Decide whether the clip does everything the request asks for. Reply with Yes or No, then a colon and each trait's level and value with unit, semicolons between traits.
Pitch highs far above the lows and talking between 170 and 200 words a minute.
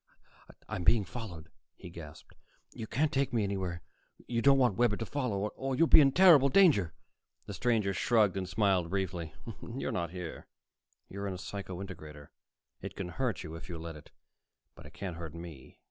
Yes: wide, 5.8 semitones; average, 185 wpm